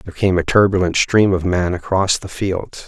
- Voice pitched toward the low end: Yes, very low, 90 Hz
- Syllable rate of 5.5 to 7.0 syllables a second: No, 5.0 syllables/s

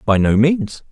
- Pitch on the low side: Yes, low, 130 Hz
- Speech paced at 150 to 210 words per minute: Yes, average, 200 wpm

